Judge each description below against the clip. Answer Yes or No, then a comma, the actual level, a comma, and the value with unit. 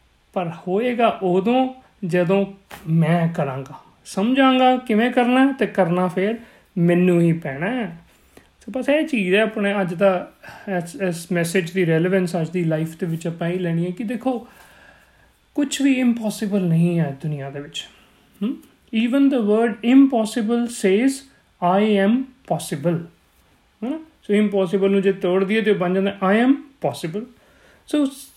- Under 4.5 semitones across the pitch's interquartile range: No, wide, 5.4 semitones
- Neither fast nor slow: Yes, average, 140 wpm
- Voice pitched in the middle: No, high, 195 Hz